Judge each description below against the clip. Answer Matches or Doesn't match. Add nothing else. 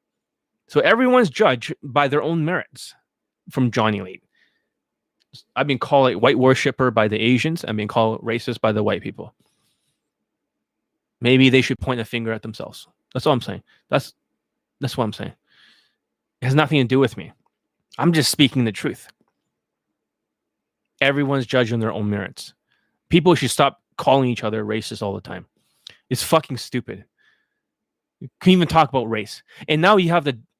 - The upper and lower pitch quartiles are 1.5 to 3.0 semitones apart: Doesn't match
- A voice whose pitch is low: Matches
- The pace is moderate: Matches